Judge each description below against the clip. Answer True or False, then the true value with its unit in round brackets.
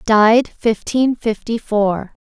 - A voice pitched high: True (220 Hz)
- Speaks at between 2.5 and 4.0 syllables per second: True (3.5 syllables/s)